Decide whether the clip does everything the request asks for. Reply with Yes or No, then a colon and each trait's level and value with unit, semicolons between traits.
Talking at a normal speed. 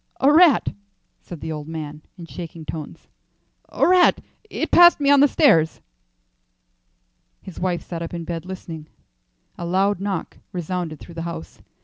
Yes: average, 155 wpm